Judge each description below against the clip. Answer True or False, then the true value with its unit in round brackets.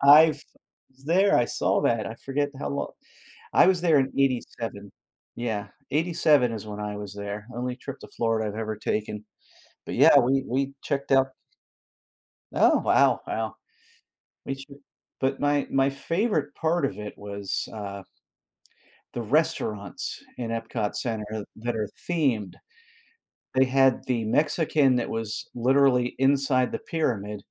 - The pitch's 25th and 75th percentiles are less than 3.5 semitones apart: False (4.6 semitones)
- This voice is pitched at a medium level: False (125 Hz)